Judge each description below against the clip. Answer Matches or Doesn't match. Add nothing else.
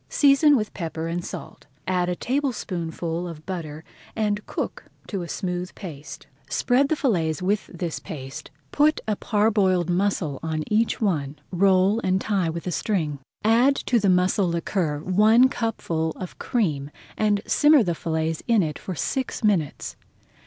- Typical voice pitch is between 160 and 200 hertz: Matches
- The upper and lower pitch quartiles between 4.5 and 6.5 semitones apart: Matches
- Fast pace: Doesn't match